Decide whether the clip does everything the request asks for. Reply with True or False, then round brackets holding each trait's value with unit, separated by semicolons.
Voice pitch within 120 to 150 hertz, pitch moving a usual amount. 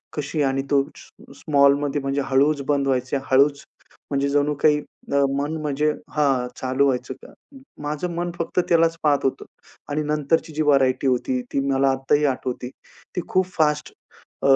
False (140 Hz; 1.9 semitones)